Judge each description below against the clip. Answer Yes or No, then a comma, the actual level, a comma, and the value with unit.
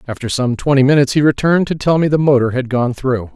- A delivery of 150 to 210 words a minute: No, fast, 250 wpm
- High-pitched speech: No, low, 135 Hz